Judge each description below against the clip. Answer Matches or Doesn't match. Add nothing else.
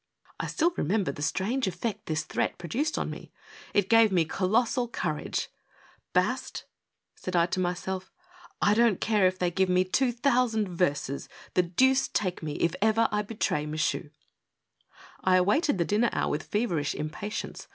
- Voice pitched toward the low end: Doesn't match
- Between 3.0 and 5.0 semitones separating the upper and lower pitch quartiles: Matches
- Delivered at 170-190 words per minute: Matches